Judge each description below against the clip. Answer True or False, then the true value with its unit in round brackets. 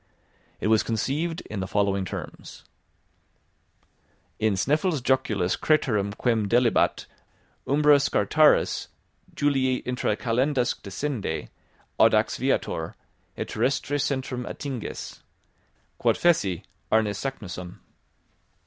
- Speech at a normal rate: False (95 wpm)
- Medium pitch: False (125 Hz)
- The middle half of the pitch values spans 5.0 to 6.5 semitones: True (5.6 semitones)